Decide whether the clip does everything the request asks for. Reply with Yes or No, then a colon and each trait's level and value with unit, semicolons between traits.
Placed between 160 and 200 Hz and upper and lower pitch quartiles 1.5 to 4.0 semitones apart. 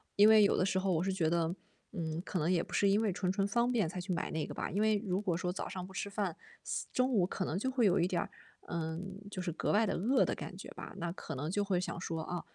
Yes: medium, 185 Hz; average, 2.9 semitones